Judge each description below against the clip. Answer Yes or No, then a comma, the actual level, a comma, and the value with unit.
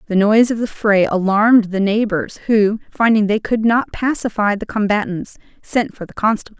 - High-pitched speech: Yes, high, 210 Hz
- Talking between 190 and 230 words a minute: No, average, 180 wpm